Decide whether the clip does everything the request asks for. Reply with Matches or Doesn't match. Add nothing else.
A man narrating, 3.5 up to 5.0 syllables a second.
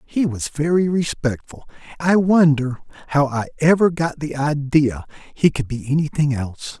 Matches